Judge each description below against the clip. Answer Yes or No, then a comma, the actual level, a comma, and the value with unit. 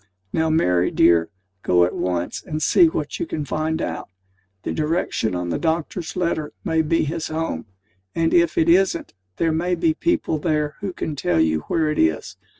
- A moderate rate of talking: Yes, average, 185 wpm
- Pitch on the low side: No, medium, 160 Hz